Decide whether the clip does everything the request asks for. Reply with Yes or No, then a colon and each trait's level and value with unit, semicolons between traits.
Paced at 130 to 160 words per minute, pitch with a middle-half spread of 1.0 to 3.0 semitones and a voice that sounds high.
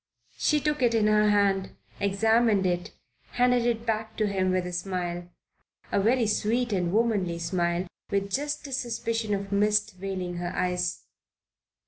No: average, 155 wpm; average, 3.8 semitones; high, 205 Hz